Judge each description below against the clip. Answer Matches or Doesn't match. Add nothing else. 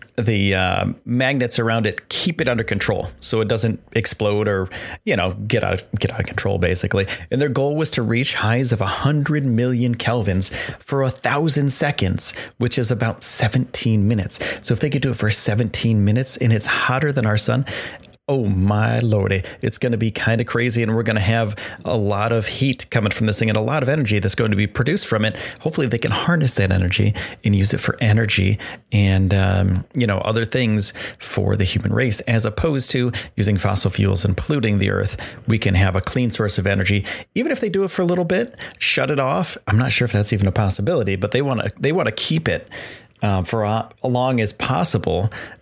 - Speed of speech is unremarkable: Doesn't match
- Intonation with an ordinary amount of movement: Matches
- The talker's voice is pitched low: Matches